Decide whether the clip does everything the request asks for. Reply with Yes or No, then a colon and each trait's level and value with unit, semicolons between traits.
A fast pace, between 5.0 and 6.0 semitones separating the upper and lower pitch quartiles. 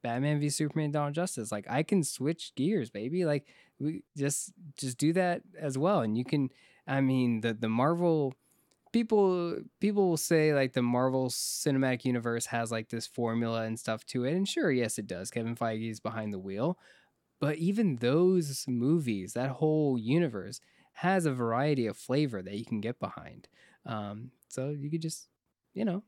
No: average, 180 wpm; wide, 5.6 semitones